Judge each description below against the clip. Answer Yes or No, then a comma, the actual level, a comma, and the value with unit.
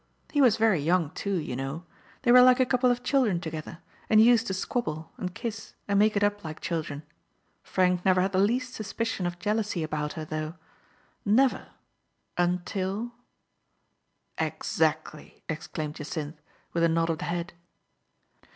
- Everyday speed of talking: Yes, average, 170 wpm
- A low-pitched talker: No, medium, 185 Hz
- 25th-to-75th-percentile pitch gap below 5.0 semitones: No, wide, 5.4 semitones